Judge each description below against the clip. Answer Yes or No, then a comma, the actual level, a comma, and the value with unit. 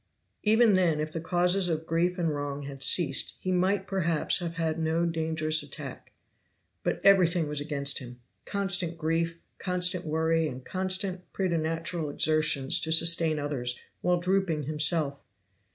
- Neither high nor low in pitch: Yes, medium, 165 Hz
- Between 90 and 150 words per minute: Yes, average, 145 wpm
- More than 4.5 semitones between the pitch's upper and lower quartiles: No, average, 2.7 semitones